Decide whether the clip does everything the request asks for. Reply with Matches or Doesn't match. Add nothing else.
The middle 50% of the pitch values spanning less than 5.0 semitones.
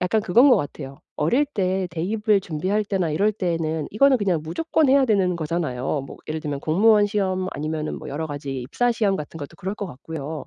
Doesn't match